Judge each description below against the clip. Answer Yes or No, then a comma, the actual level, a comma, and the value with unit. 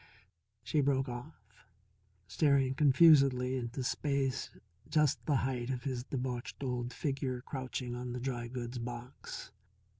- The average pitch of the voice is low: Yes, low, 130 Hz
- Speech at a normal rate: No, slow, 125 wpm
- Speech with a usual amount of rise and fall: No, narrow, 2.0 semitones